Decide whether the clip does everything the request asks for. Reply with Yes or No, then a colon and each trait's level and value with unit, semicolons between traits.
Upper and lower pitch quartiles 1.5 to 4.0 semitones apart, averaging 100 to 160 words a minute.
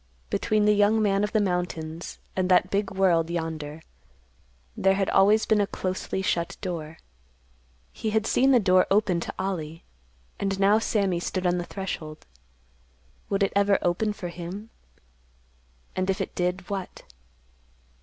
Yes: average, 2.7 semitones; average, 155 wpm